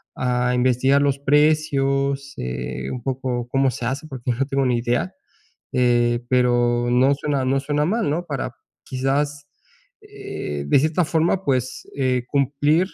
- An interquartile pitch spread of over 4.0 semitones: No, average, 2.8 semitones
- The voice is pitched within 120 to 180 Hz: Yes, low, 135 Hz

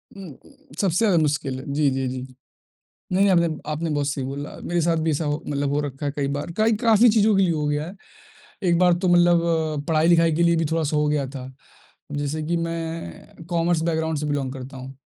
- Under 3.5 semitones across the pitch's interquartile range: Yes, average, 2.9 semitones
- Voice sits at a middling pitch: Yes, medium, 160 Hz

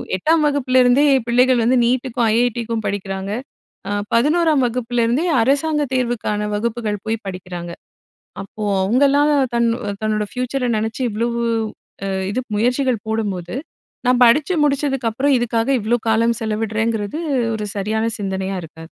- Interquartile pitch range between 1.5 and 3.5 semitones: Yes, average, 3.2 semitones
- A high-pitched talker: Yes, high, 235 Hz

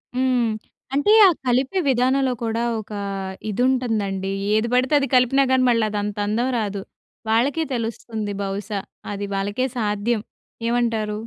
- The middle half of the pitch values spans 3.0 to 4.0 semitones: Yes, average, 3.5 semitones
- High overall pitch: Yes, high, 230 Hz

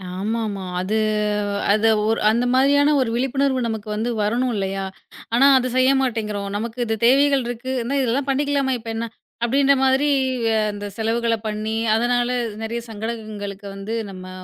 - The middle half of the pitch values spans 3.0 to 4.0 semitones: Yes, average, 3.5 semitones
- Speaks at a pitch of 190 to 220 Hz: No, high, 230 Hz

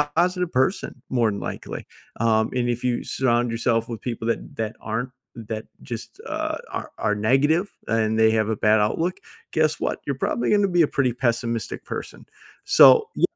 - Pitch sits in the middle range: No, low, 120 Hz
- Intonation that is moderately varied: Yes, average, 3.2 semitones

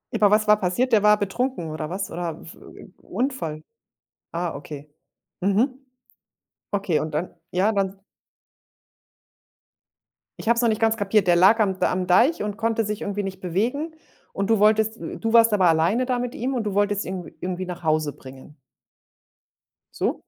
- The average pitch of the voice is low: No, high, 200 Hz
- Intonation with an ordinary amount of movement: Yes, average, 4.1 semitones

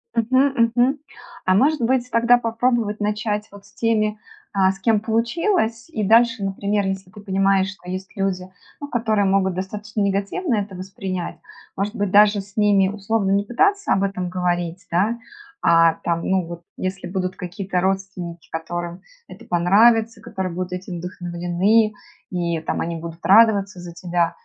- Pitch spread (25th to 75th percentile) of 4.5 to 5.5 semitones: No, average, 3.3 semitones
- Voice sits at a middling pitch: No, high, 195 Hz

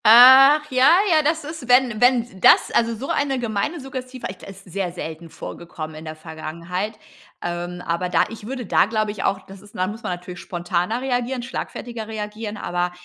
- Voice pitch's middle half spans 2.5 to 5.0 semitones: No, wide, 5.9 semitones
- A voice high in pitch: Yes, high, 215 Hz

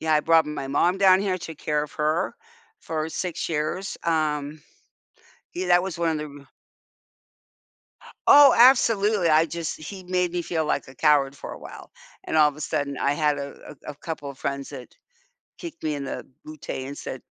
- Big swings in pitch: No, average, 3.2 semitones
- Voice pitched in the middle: Yes, medium, 155 Hz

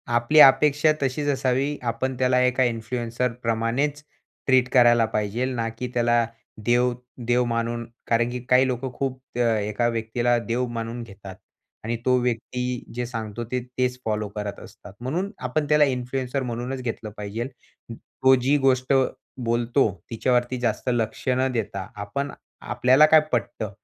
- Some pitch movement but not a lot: No, narrow, 2.0 semitones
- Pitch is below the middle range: Yes, low, 120 Hz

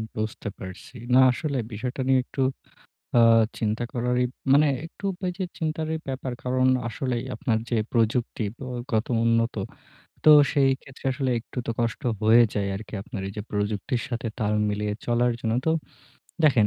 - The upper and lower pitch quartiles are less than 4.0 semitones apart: Yes, average, 3.4 semitones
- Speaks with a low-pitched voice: Yes, low, 120 Hz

